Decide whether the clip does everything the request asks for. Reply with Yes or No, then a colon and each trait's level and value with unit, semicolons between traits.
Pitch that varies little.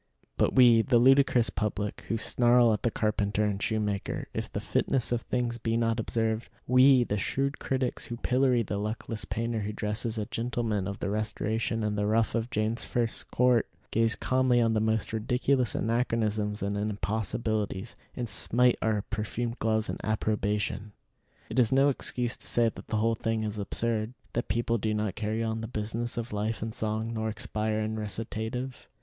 Yes: narrow, 1.9 semitones